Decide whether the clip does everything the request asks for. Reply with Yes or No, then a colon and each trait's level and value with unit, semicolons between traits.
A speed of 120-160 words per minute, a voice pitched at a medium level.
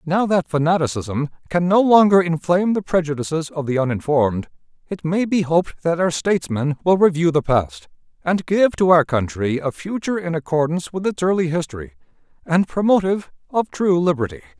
No: average, 170 wpm; medium, 165 Hz